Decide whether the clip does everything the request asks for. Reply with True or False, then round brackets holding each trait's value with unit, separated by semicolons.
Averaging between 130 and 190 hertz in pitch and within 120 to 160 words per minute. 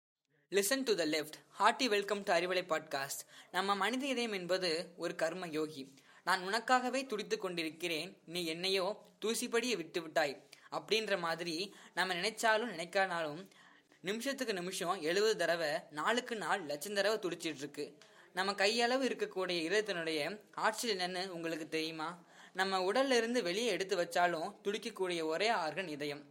True (185 Hz; 125 wpm)